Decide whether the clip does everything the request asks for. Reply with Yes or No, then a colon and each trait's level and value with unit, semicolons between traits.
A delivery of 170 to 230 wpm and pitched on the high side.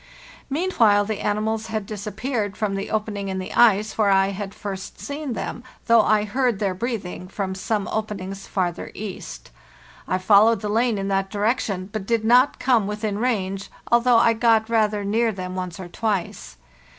Yes: average, 175 wpm; high, 210 Hz